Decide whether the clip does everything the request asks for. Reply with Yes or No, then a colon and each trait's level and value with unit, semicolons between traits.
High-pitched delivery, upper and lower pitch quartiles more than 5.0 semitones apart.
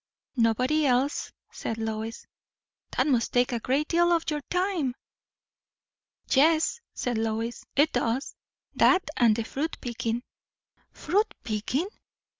Yes: very high, 255 Hz; wide, 5.4 semitones